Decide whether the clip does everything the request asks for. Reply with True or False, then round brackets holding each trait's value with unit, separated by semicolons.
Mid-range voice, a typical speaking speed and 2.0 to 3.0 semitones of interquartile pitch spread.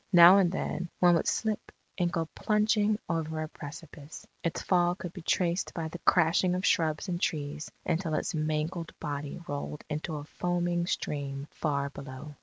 True (165 Hz; 170 wpm; 2.7 semitones)